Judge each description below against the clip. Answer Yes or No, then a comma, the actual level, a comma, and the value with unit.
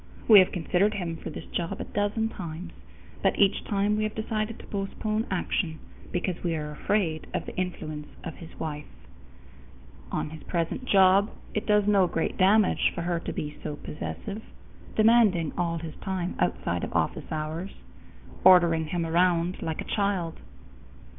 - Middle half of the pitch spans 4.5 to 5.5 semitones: No, average, 3.8 semitones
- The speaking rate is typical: Yes, average, 165 wpm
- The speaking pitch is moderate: Yes, medium, 180 Hz